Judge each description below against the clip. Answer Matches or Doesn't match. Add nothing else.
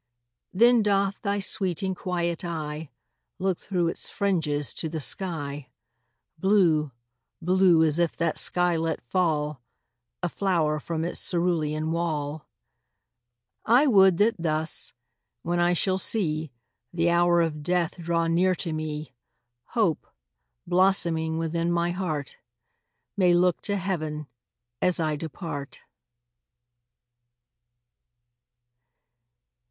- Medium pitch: Matches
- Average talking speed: Doesn't match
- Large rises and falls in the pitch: Doesn't match